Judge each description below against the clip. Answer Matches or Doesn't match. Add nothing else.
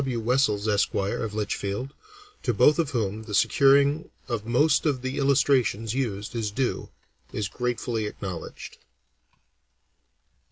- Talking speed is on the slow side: Matches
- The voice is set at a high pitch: Doesn't match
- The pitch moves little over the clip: Doesn't match